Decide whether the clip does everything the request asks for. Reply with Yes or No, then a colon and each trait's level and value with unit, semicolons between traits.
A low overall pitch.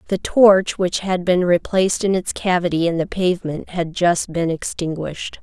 No: medium, 175 Hz